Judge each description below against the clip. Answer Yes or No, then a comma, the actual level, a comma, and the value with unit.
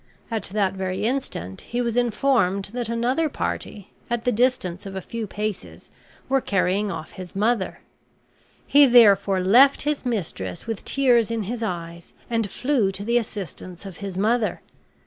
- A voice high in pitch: Yes, high, 215 Hz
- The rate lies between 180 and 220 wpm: No, average, 160 wpm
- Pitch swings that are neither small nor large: Yes, average, 4.1 semitones